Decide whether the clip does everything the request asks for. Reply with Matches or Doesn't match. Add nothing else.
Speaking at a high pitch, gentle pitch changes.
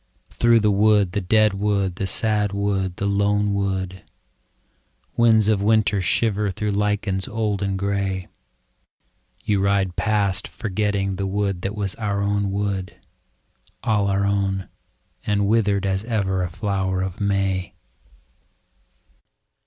Doesn't match